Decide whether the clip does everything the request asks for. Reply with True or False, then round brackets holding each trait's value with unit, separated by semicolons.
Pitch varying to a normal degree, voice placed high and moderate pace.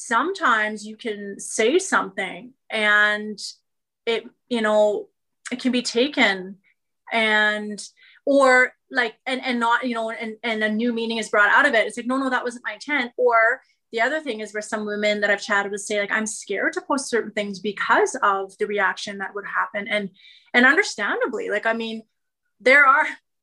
True (3.1 semitones; 225 Hz; 190 wpm)